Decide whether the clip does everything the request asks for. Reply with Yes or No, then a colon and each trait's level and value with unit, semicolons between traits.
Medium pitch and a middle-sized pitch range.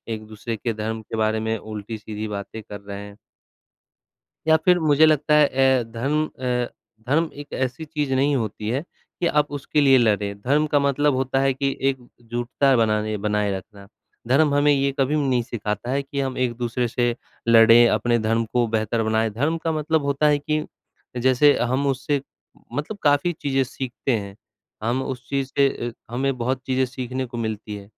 No: low, 130 Hz; average, 4.0 semitones